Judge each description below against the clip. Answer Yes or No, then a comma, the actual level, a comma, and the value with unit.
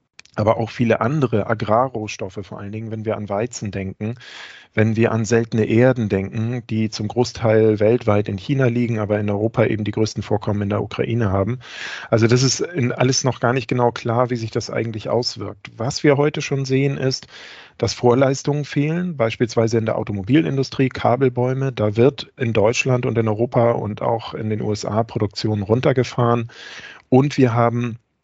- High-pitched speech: No, low, 115 Hz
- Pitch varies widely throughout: No, average, 2.8 semitones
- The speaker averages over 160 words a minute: Yes, average, 175 wpm